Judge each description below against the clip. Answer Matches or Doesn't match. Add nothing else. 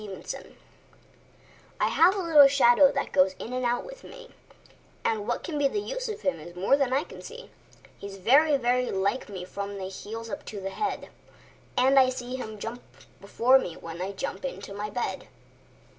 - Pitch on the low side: Doesn't match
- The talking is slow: Doesn't match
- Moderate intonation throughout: Doesn't match